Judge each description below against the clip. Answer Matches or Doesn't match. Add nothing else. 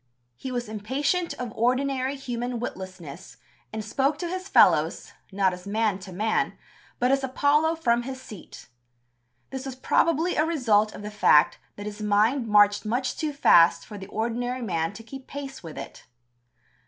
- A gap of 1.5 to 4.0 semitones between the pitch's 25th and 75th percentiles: Doesn't match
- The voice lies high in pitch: Matches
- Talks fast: Doesn't match